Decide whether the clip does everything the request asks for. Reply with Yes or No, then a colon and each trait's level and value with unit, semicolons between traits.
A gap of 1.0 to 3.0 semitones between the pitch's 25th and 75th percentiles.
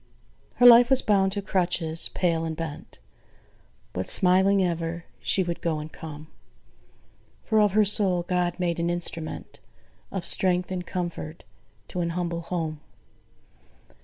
Yes: narrow, 2.4 semitones